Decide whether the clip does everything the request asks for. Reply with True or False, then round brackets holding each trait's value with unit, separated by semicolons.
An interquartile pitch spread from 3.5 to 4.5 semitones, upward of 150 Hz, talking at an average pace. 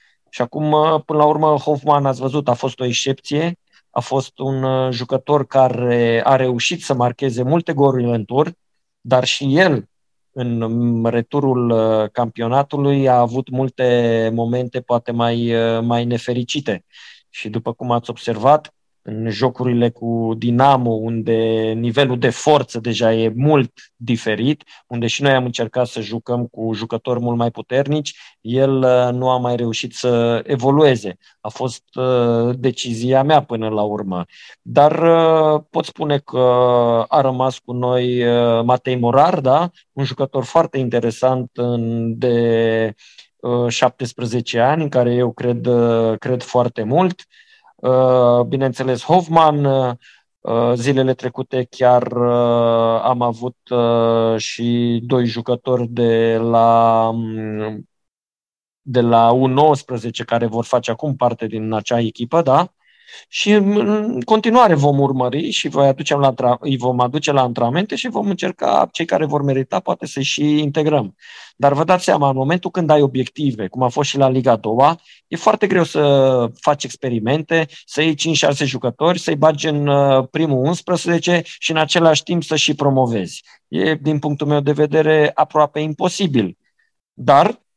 False (3.9 semitones; 130 Hz; 135 wpm)